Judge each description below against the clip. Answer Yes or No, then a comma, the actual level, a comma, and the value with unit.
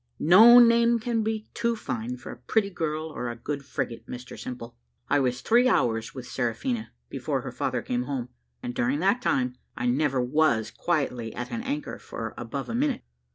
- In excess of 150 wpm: Yes, average, 190 wpm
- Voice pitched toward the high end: No, medium, 150 Hz